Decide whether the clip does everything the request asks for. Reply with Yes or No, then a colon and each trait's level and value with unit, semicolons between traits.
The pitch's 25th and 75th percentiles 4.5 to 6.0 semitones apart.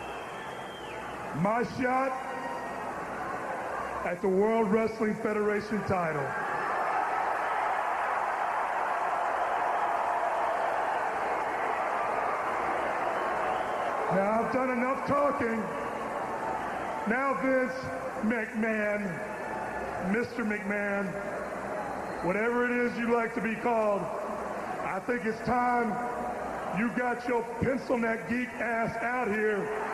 No: narrow, 2.6 semitones